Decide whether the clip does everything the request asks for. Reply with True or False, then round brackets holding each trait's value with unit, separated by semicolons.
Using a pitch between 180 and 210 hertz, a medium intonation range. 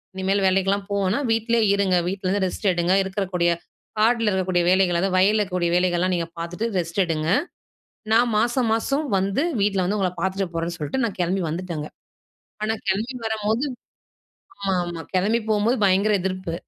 True (190 Hz; 3.0 semitones)